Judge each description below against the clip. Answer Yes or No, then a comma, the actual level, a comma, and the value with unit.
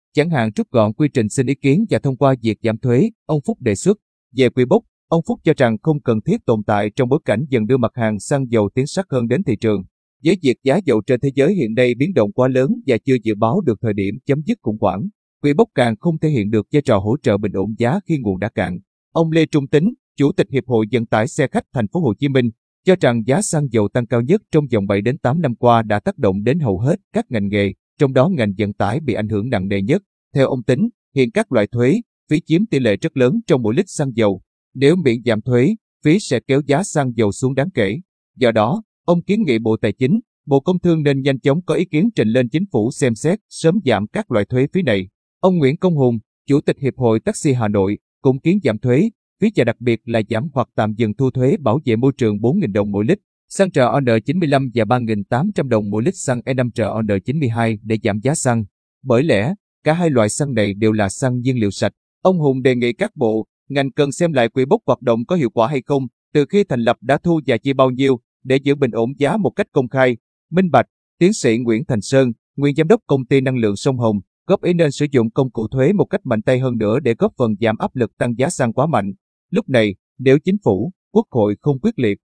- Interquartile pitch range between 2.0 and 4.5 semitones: No, wide, 5.4 semitones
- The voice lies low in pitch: Yes, low, 130 Hz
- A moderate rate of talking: No, fast, 255 wpm